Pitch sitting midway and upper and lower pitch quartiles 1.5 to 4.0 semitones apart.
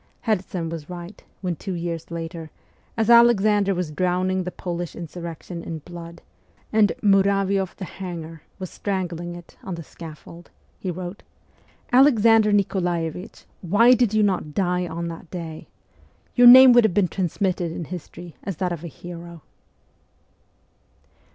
Yes: medium, 180 Hz; average, 2.9 semitones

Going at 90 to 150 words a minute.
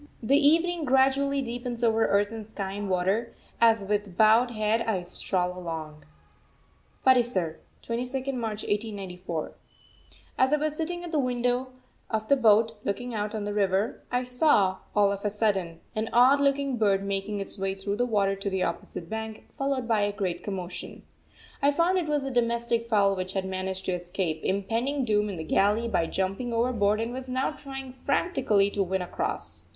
No: average, 180 wpm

